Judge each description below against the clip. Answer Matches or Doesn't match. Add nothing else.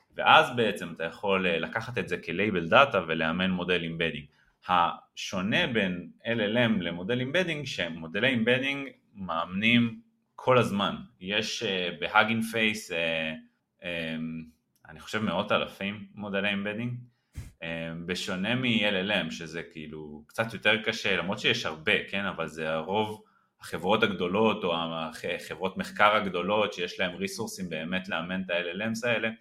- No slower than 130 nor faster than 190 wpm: Doesn't match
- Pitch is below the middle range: Matches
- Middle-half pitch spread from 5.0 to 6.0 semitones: Matches